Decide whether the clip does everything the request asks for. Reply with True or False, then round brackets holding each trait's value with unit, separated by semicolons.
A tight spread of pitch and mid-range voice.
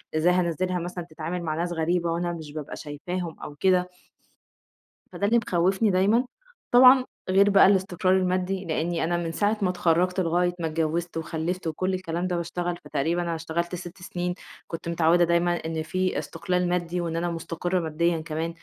True (1.8 semitones; 175 Hz)